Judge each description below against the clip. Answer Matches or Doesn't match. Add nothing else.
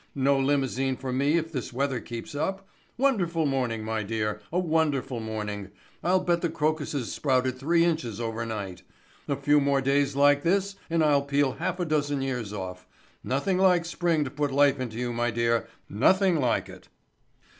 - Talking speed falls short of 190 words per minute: Matches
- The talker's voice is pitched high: Doesn't match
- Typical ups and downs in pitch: Matches